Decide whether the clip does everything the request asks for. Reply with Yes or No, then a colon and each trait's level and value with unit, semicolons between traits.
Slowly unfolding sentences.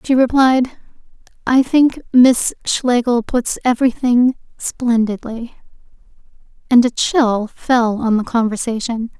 Yes: slow, 105 wpm